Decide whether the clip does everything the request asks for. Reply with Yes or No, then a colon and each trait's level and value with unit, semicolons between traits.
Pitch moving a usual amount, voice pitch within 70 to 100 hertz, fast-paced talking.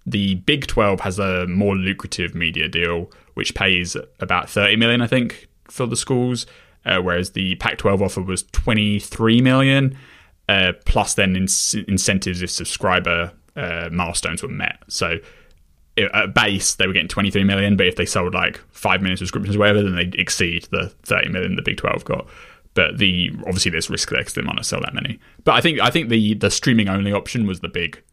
No: average, 3.0 semitones; very low, 95 Hz; average, 195 wpm